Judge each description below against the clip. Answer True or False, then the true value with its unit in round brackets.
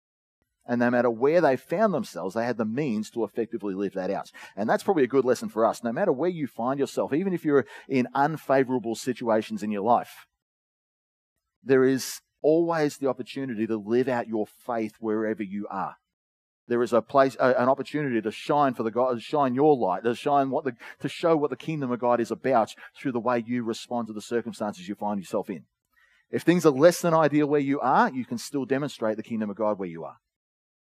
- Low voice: True (120 Hz)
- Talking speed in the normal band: False (220 wpm)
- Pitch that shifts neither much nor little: True (4.4 semitones)